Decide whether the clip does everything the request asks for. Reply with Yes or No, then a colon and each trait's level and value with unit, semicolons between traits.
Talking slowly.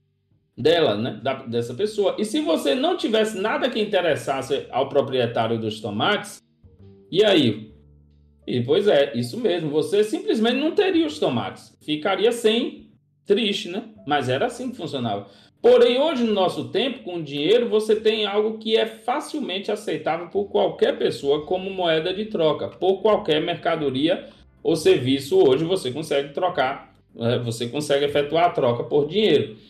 No: average, 155 wpm